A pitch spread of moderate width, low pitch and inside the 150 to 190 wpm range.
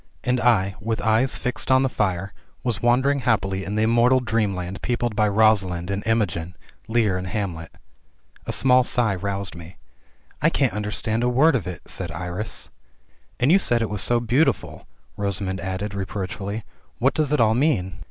Yes: average, 4.1 semitones; low, 105 Hz; average, 180 wpm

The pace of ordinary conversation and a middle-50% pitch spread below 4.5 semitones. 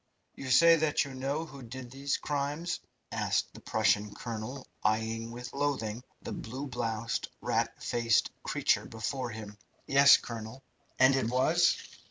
Yes: average, 145 wpm; average, 3.6 semitones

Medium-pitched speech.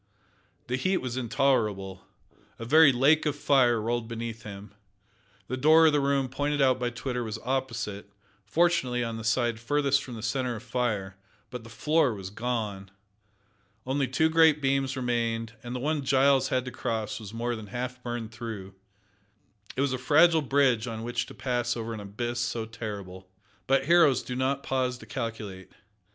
No: low, 125 Hz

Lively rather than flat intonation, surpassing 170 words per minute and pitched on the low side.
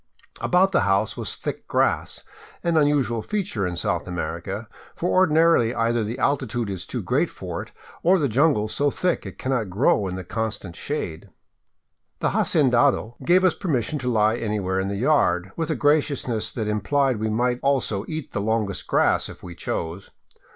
Yes: wide, 6.4 semitones; average, 180 wpm; low, 115 Hz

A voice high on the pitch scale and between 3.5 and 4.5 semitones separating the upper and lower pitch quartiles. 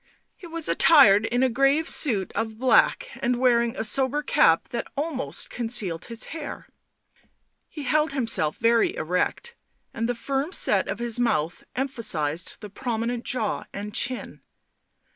Yes: high, 240 Hz; average, 4.2 semitones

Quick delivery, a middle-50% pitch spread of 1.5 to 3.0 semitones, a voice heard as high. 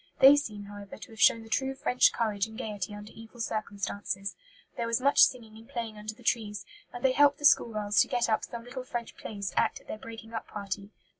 Yes: fast, 235 wpm; average, 2.7 semitones; high, 225 Hz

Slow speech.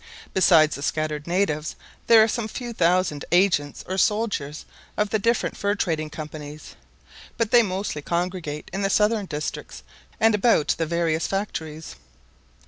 No: average, 145 wpm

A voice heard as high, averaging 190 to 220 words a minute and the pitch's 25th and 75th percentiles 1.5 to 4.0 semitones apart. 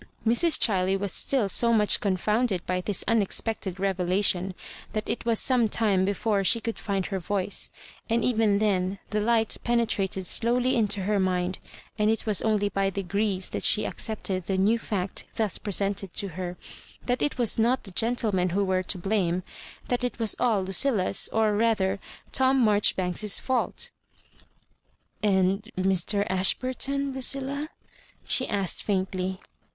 No: high, 205 Hz; average, 155 wpm; average, 3.2 semitones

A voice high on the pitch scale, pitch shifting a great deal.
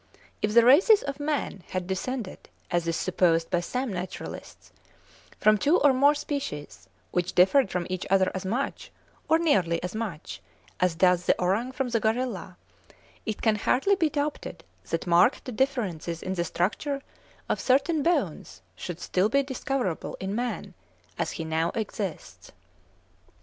Yes: high, 210 Hz; wide, 7.2 semitones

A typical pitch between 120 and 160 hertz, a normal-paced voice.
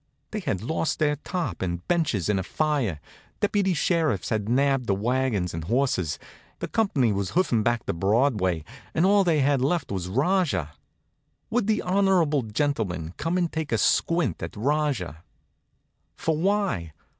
Yes: low, 135 Hz; average, 155 wpm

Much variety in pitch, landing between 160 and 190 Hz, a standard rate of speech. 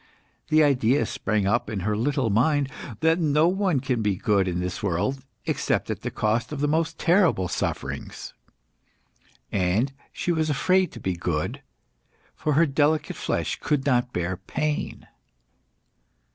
No: wide, 7.1 semitones; low, 130 Hz; average, 150 wpm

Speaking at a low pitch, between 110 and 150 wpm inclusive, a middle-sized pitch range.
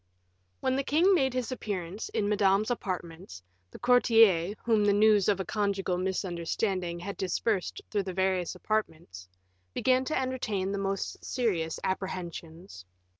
No: high, 195 Hz; average, 140 wpm; average, 3.6 semitones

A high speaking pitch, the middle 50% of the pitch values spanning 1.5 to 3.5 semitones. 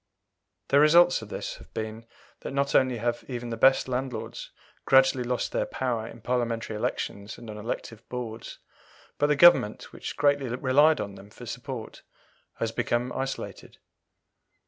No: low, 125 Hz; average, 2.9 semitones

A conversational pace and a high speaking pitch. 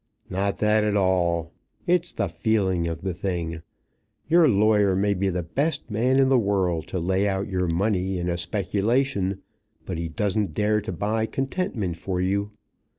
No: average, 170 wpm; low, 100 Hz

